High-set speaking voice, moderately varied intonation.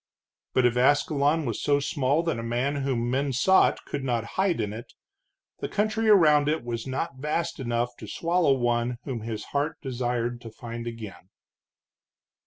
No: low, 130 Hz; average, 3.9 semitones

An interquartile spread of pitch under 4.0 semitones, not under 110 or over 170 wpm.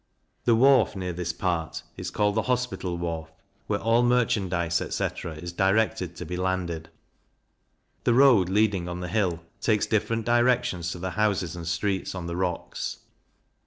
No: average, 4.3 semitones; average, 160 wpm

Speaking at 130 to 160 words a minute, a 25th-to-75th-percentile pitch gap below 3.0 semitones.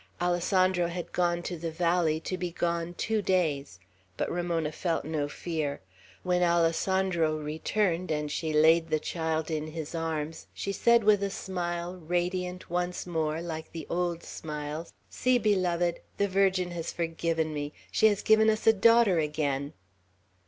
Yes: average, 155 wpm; narrow, 2.4 semitones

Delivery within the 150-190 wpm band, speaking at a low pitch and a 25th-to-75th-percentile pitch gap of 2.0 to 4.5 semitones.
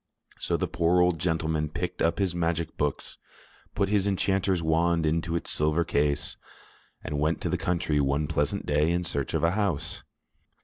Yes: average, 175 wpm; very low, 85 Hz; narrow, 2.6 semitones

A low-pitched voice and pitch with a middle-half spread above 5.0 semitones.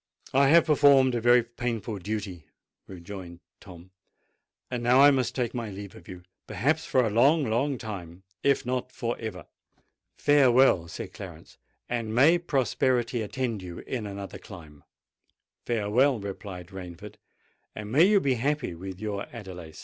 Yes: low, 115 Hz; wide, 5.4 semitones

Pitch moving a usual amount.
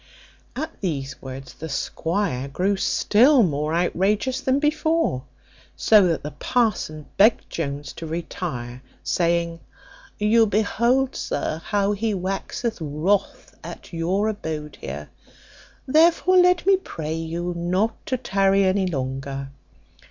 No: wide, 6.4 semitones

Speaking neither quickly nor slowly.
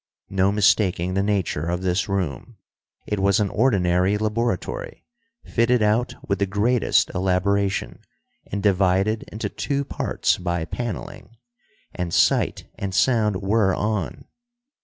No: slow, 125 wpm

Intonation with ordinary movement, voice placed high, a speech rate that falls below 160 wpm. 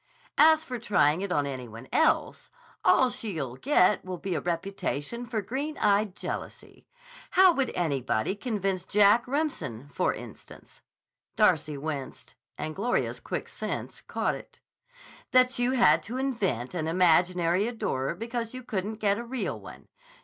No: wide, 7.4 semitones; high, 200 Hz; average, 150 wpm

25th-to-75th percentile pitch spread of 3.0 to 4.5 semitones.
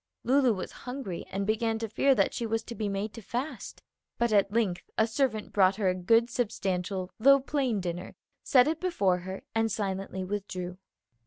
Yes: average, 3.9 semitones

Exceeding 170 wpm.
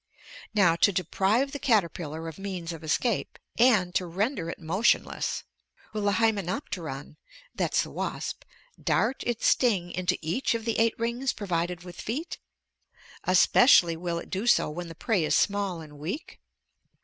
No: average, 155 wpm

